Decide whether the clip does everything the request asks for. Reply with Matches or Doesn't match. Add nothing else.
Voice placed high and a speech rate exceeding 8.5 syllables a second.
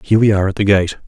Doesn't match